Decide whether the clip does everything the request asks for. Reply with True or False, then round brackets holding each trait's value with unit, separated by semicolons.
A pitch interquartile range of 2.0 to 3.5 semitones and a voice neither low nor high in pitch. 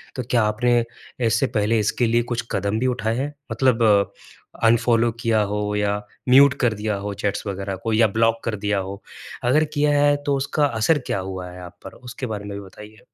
False (3.1 semitones; 115 Hz)